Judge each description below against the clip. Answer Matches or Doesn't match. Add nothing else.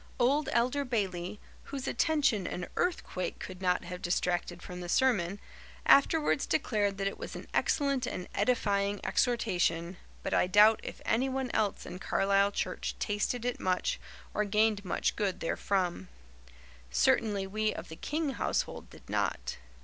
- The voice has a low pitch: Doesn't match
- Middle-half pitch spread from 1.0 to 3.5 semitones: Doesn't match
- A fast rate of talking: Doesn't match